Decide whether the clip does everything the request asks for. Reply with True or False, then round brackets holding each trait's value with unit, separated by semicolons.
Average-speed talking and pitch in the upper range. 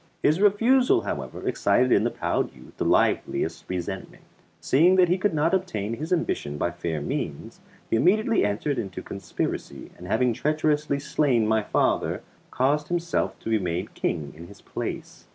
False (165 wpm; 130 Hz)